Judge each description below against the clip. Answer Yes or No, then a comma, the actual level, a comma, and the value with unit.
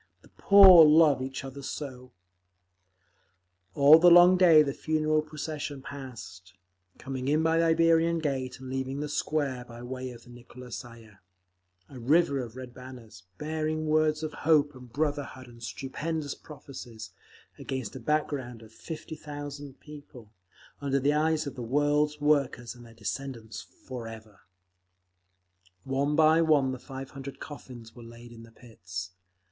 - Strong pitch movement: No, average, 3.9 semitones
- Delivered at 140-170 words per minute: Yes, average, 150 wpm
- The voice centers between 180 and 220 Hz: No, low, 135 Hz